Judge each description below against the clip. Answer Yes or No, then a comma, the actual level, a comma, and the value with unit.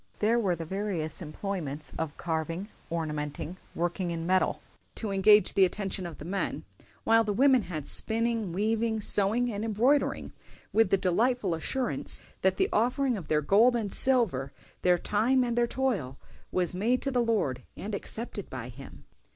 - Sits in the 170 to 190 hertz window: No, high, 200 Hz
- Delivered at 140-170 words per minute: Yes, average, 165 wpm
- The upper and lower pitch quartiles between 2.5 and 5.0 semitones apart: No, wide, 5.4 semitones